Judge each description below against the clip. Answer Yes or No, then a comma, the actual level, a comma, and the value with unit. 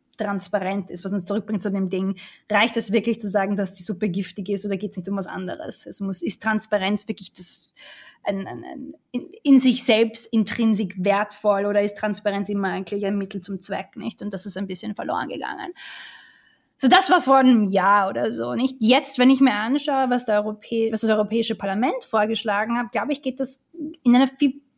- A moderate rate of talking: No, fast, 215 wpm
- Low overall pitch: No, high, 210 Hz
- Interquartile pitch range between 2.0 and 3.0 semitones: No, average, 3.7 semitones